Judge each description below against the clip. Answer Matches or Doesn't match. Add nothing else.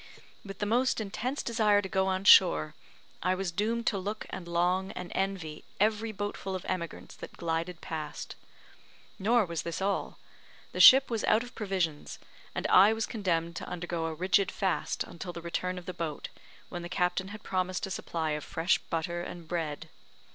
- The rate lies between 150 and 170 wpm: Doesn't match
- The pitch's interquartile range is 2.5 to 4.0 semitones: Matches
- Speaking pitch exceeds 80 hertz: Matches